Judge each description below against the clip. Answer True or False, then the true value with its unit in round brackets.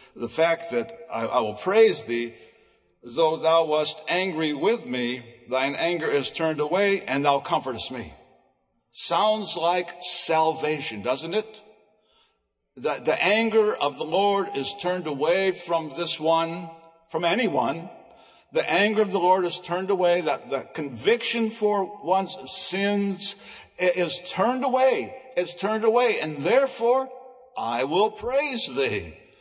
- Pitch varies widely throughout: False (5.0 semitones)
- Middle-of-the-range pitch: True (180 Hz)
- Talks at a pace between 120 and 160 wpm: True (140 wpm)